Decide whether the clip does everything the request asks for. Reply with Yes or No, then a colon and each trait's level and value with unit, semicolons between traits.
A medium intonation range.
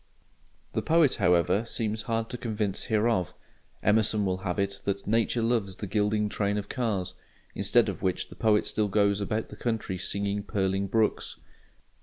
No: narrow, 2.2 semitones